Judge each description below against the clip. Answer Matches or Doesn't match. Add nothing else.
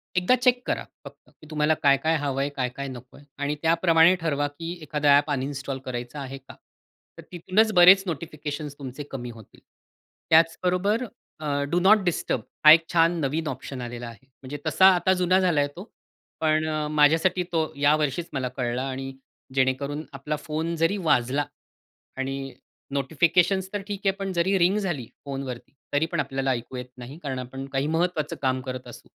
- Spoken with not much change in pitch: Doesn't match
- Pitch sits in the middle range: Matches